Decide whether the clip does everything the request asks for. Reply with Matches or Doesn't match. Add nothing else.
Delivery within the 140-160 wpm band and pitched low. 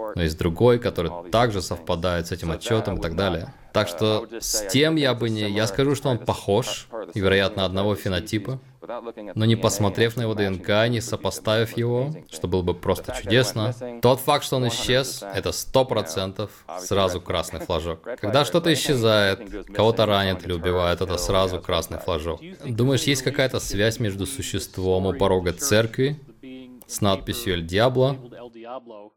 Matches